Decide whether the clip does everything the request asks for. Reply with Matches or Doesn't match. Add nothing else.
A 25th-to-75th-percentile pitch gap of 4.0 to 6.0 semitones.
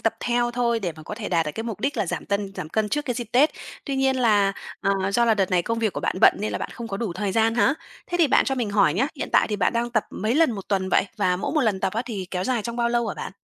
Doesn't match